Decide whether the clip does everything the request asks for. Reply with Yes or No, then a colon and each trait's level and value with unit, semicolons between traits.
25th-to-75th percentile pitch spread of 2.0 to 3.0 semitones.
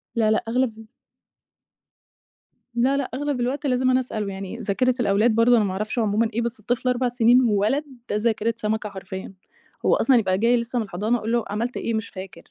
Yes: average, 2.7 semitones